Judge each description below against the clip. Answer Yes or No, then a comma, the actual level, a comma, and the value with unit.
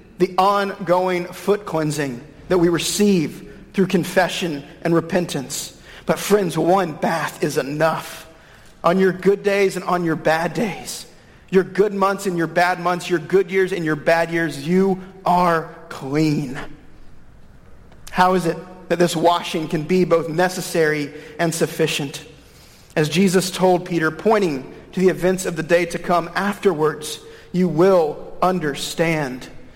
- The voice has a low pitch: No, medium, 175 Hz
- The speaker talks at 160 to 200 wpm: No, average, 145 wpm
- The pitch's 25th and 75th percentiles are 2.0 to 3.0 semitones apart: Yes, narrow, 2.6 semitones